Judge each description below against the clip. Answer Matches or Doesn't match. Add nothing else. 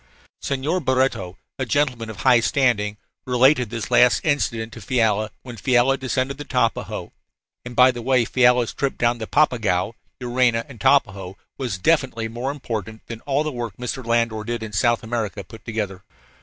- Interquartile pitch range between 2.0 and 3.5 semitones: Matches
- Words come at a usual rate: Matches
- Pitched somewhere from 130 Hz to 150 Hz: Doesn't match